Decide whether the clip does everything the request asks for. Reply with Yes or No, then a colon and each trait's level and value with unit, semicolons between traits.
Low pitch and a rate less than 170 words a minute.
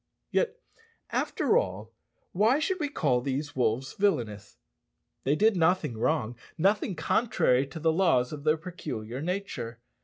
No: medium, 155 Hz; average, 140 wpm